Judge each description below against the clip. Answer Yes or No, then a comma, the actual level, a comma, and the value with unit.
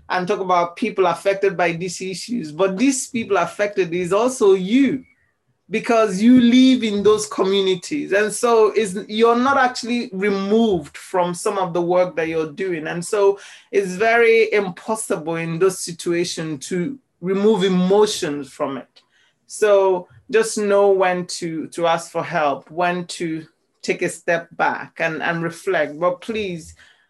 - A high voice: Yes, high, 195 Hz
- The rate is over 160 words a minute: No, average, 155 wpm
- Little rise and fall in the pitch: No, average, 3.8 semitones